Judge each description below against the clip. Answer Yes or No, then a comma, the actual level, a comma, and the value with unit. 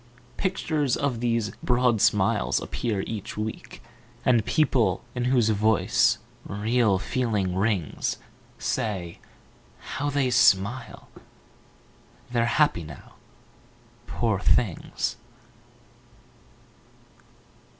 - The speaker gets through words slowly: Yes, slow, 85 wpm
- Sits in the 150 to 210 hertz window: No, low, 115 Hz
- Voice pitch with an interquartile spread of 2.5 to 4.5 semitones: Yes, average, 3.8 semitones